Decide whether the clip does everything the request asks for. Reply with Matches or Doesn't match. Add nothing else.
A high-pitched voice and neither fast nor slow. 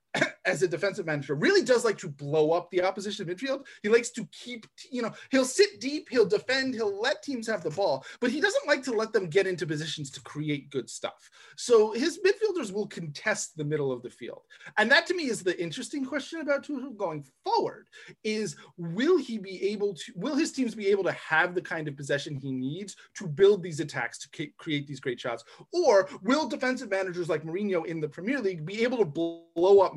Doesn't match